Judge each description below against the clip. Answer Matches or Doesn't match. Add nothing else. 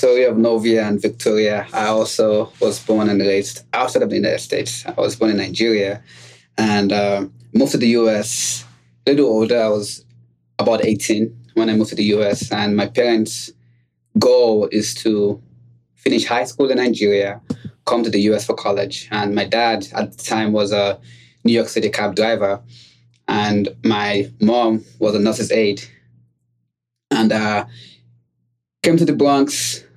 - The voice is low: Matches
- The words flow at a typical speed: Matches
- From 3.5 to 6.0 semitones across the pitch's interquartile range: Doesn't match